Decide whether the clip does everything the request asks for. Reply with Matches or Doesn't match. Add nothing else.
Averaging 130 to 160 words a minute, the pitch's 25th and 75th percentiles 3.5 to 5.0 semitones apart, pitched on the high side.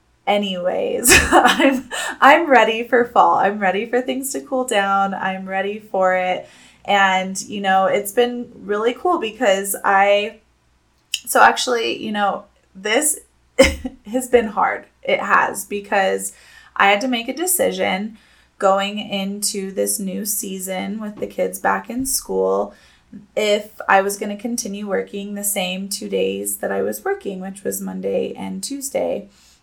Matches